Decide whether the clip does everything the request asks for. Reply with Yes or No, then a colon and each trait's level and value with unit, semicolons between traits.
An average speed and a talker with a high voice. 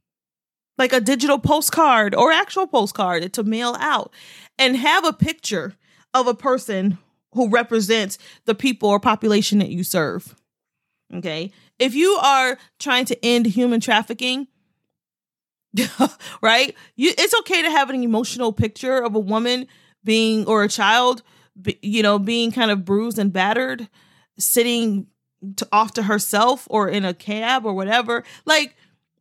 Yes: average, 145 wpm; high, 230 Hz